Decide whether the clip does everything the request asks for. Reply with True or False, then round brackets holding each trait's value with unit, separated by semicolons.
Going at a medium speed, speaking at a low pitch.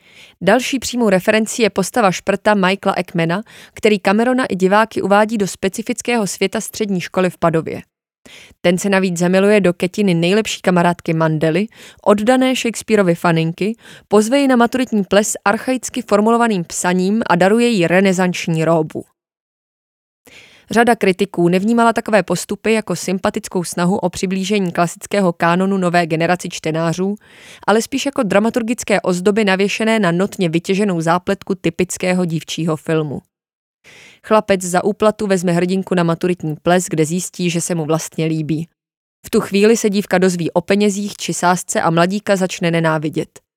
False (140 wpm; 190 Hz)